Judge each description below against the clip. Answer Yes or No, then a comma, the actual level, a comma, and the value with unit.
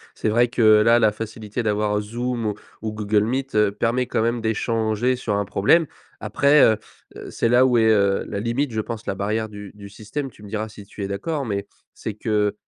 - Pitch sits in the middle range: No, low, 110 Hz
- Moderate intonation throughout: No, narrow, 2.3 semitones